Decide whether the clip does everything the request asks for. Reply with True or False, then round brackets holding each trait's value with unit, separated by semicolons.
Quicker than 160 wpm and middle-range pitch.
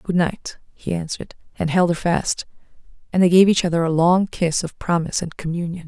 True (205 wpm; 170 Hz)